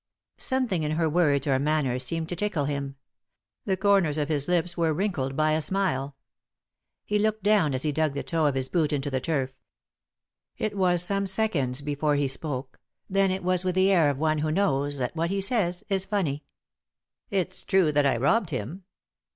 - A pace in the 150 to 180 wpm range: No, average, 200 wpm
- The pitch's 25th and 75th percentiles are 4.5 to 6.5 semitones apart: Yes, average, 5.0 semitones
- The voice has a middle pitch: Yes, medium, 160 Hz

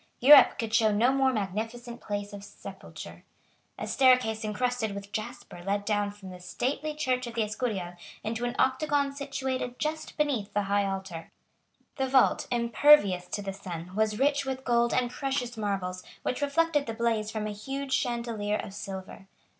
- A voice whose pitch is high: Yes, high, 230 Hz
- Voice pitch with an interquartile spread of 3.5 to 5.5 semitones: Yes, average, 4.5 semitones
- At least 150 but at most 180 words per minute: Yes, average, 170 wpm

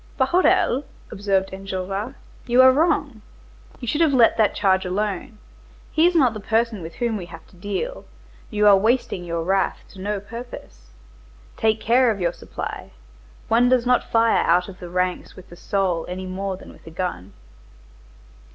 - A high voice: Yes, high, 205 Hz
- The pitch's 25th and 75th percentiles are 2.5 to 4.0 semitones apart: No, average, 4.6 semitones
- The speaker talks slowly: No, average, 175 wpm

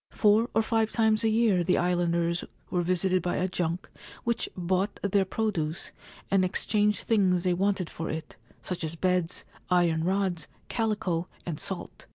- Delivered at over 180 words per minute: No, average, 165 wpm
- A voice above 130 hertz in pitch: Yes, medium, 185 Hz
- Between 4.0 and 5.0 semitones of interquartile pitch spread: No, average, 3.1 semitones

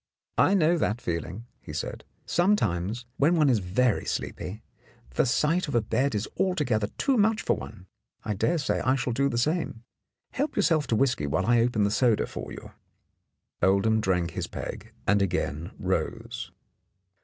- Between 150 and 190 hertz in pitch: No, low, 120 Hz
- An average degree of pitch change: No, wide, 7.2 semitones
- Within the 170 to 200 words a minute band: Yes, average, 175 wpm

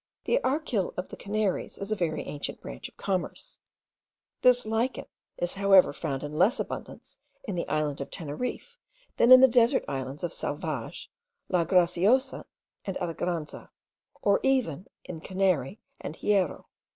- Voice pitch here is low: No, medium, 185 Hz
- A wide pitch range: Yes, wide, 6.1 semitones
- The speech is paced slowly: No, average, 150 wpm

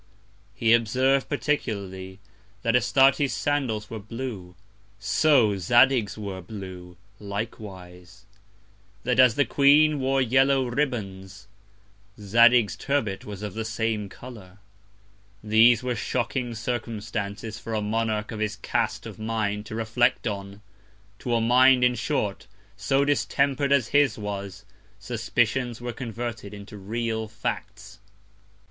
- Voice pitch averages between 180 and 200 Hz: No, low, 115 Hz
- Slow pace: Yes, slow, 120 wpm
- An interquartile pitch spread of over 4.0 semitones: No, average, 3.4 semitones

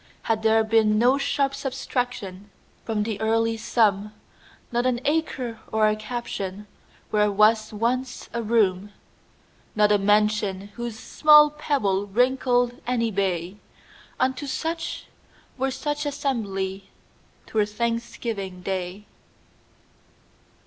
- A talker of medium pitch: No, high, 220 Hz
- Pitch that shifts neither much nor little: Yes, average, 3.4 semitones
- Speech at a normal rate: No, slow, 95 wpm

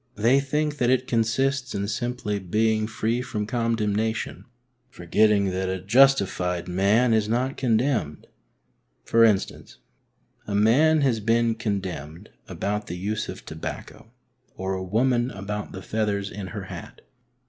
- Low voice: Yes, low, 110 Hz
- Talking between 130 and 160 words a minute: Yes, slow, 135 wpm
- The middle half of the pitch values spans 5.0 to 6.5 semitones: No, average, 3.4 semitones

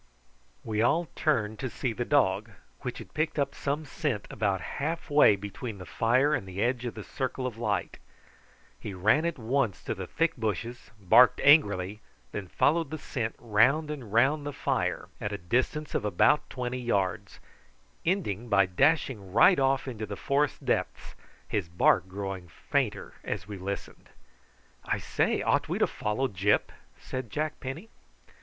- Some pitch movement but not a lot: No, wide, 5.7 semitones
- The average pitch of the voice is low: Yes, low, 120 Hz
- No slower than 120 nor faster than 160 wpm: No, average, 170 wpm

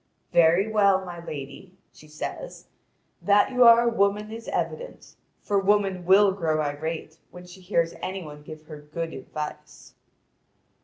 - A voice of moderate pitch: Yes, medium, 180 Hz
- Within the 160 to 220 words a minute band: No, average, 150 wpm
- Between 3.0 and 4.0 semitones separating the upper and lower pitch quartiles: No, average, 4.6 semitones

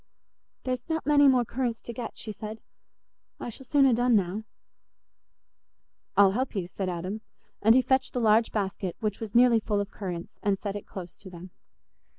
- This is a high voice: Yes, high, 220 Hz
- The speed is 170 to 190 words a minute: Yes, average, 185 wpm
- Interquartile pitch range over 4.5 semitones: No, average, 4.0 semitones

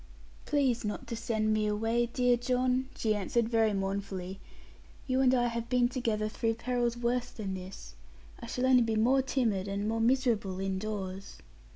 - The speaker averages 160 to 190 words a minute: Yes, average, 170 wpm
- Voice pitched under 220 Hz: No, high, 230 Hz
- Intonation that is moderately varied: Yes, average, 3.1 semitones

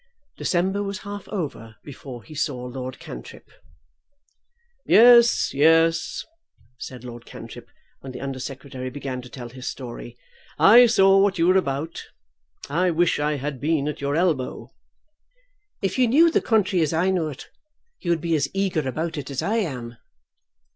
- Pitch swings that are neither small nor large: No, wide, 6.3 semitones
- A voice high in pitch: No, medium, 155 Hz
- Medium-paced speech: Yes, average, 160 wpm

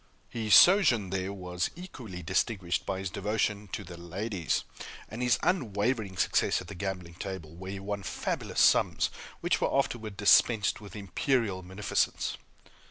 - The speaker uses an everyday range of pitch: Yes, average, 3.1 semitones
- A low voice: Yes, low, 100 Hz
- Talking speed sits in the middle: Yes, average, 150 wpm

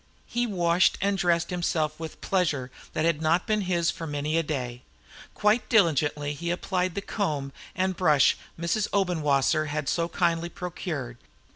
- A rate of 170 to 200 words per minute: No, average, 160 wpm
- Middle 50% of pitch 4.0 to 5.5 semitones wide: No, average, 3.6 semitones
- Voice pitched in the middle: Yes, medium, 170 Hz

